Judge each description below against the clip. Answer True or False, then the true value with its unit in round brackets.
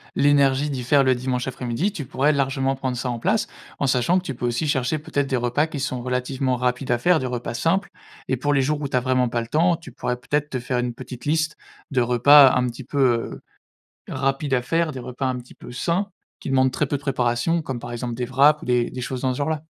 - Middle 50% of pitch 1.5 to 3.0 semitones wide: True (2.7 semitones)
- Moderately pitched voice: False (130 Hz)